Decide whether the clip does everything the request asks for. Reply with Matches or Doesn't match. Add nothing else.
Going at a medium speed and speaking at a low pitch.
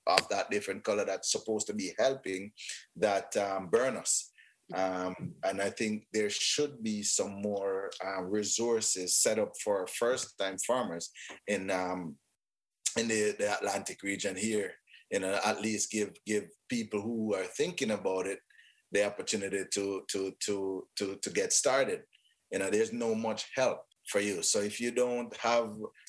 Matches